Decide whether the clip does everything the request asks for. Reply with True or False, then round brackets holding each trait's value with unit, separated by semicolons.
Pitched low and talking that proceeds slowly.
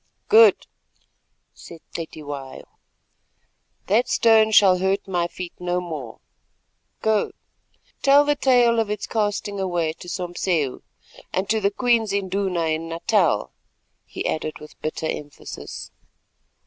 False (185 Hz; 120 wpm)